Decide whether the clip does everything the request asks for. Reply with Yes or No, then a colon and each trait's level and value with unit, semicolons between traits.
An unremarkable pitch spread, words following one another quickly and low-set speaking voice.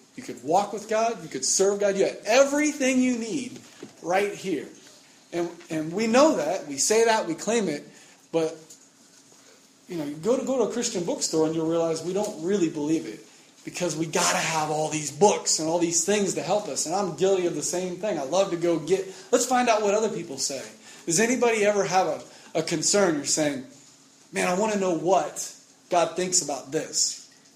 No: average, 4.8 semitones; fast, 215 wpm; medium, 185 Hz